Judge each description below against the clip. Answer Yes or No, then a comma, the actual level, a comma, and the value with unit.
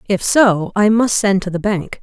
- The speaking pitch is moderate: No, high, 200 Hz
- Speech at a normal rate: No, fast, 235 wpm